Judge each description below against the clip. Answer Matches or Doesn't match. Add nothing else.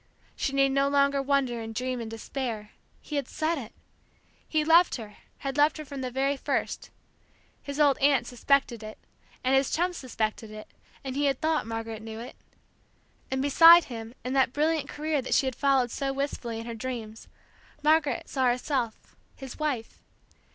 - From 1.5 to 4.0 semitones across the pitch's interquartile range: Matches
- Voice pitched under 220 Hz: Doesn't match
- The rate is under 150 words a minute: Doesn't match